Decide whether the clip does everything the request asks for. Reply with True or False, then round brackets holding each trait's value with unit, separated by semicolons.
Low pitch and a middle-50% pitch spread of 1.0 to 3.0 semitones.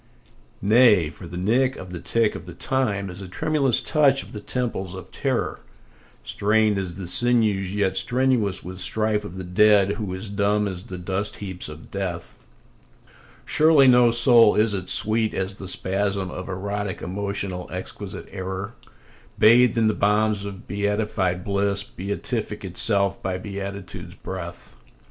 True (100 Hz; 2.7 semitones)